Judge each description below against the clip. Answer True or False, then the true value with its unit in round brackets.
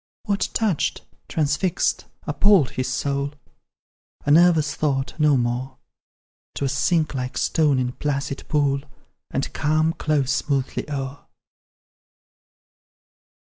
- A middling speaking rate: False (105 wpm)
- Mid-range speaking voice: True (145 Hz)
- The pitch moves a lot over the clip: False (2.5 semitones)